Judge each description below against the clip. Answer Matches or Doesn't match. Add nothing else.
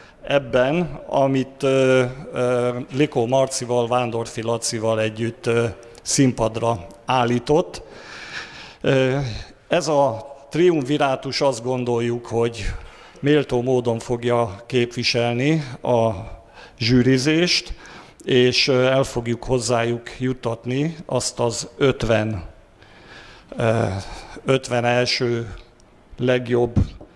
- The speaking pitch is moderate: Doesn't match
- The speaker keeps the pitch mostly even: Matches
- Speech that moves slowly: Matches